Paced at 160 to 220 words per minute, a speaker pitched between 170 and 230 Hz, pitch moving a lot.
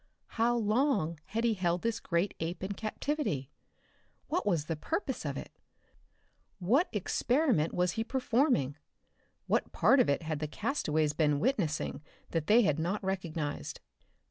No: average, 145 wpm; high, 190 Hz; wide, 7.0 semitones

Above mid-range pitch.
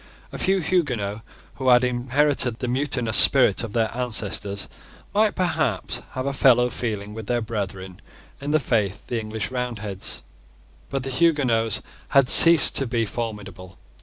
No: low, 120 Hz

